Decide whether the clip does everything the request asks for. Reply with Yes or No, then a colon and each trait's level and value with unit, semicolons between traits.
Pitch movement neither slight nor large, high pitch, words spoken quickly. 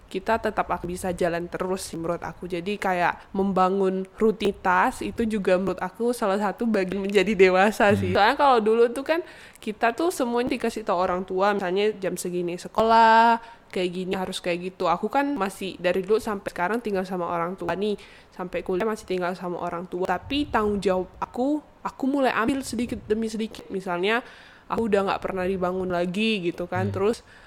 Yes: average, 3.5 semitones; high, 195 Hz; fast, 180 wpm